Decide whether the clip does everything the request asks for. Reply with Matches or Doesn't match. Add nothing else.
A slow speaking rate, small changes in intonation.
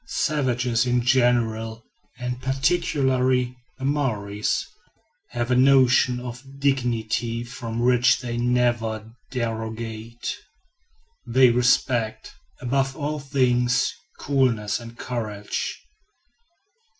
Matches